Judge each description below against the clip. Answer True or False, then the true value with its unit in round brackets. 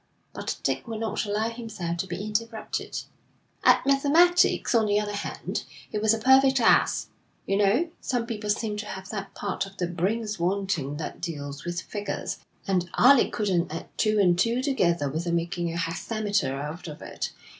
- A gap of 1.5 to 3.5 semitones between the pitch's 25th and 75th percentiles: False (4.5 semitones)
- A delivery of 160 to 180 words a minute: True (175 wpm)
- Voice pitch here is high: True (205 Hz)